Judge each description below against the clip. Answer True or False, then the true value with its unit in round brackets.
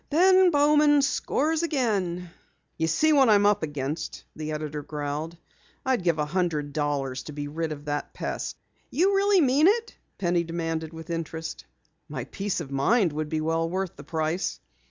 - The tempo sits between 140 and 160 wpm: False (170 wpm)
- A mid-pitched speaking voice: True (165 Hz)